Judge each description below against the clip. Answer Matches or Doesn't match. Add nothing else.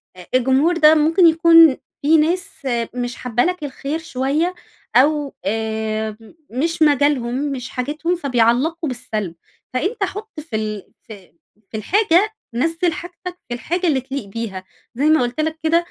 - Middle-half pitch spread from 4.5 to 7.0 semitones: Matches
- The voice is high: Matches